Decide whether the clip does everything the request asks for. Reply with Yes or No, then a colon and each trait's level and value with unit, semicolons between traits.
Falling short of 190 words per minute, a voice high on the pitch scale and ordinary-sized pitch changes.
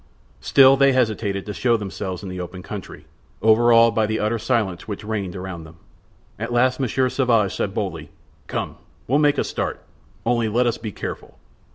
No: average, 180 wpm; low, 110 Hz; average, 3.6 semitones